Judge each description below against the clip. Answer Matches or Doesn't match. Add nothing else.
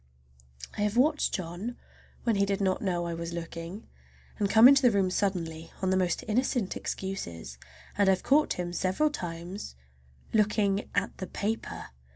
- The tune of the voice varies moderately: Matches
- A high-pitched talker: Matches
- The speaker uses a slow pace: Doesn't match